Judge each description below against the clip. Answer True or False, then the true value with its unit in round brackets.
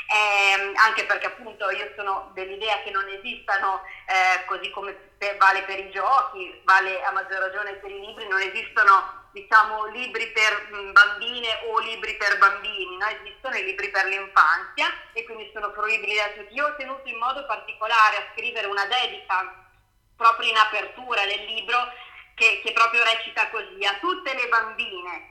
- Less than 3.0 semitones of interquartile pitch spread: True (2.5 semitones)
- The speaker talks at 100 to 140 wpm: False (165 wpm)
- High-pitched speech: True (210 Hz)